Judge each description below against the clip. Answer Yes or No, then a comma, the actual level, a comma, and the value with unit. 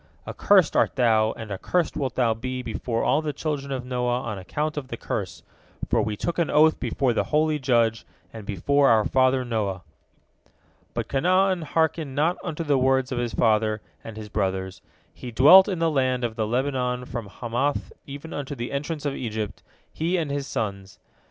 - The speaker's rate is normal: Yes, average, 185 wpm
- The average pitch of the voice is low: Yes, low, 130 Hz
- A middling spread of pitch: Yes, average, 4.7 semitones